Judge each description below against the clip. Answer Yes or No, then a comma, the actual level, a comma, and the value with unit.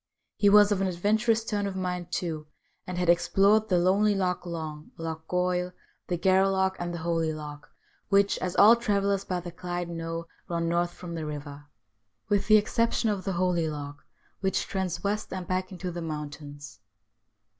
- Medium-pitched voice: Yes, medium, 180 Hz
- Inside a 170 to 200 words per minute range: Yes, average, 175 wpm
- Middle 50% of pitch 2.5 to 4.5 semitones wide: Yes, average, 3.0 semitones